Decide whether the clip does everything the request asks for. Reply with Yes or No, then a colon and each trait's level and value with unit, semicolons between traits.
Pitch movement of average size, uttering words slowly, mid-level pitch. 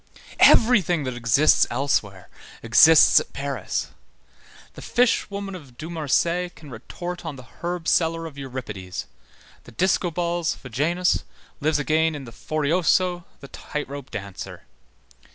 Yes: average, 4.9 semitones; slow, 120 wpm; medium, 155 Hz